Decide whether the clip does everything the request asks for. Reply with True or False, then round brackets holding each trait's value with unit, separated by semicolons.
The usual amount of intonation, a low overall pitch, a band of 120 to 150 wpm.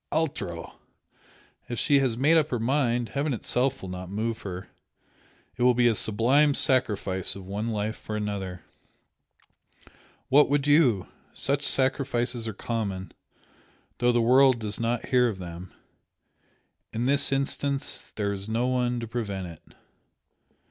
True (4.6 semitones; 120 Hz; 145 wpm)